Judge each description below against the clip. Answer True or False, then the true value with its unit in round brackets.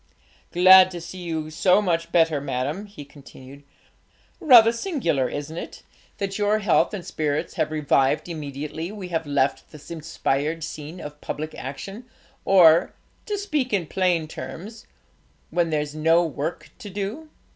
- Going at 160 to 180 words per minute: False (145 wpm)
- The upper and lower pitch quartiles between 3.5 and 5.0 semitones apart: True (4.6 semitones)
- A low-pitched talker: False (165 Hz)